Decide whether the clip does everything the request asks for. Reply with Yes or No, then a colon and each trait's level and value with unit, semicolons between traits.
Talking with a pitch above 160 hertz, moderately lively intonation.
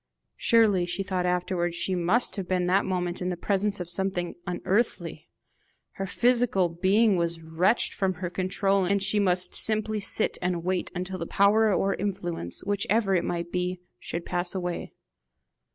No: medium, 185 Hz; narrow, 2.1 semitones